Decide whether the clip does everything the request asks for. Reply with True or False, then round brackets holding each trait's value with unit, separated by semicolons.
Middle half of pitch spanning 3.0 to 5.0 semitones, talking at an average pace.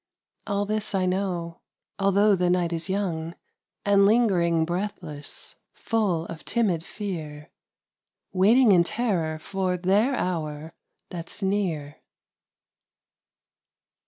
False (3.4 semitones; 100 wpm)